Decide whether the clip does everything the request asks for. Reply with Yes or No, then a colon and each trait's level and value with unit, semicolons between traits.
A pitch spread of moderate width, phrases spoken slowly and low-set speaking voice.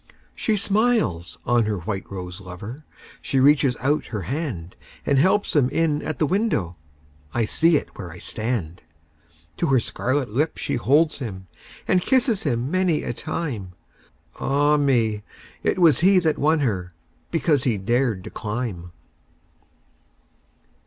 No: wide, 8.8 semitones; slow, 125 wpm; low, 125 Hz